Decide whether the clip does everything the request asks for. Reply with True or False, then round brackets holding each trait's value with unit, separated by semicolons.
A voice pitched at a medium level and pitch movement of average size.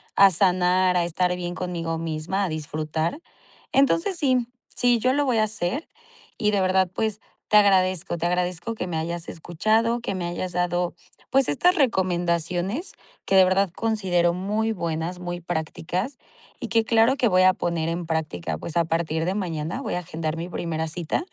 True (180 Hz; 4.0 semitones)